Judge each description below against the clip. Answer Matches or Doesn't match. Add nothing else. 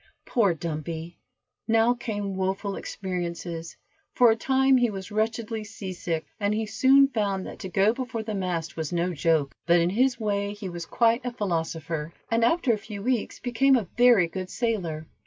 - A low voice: Doesn't match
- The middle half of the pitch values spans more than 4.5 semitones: Matches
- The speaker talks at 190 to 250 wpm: Doesn't match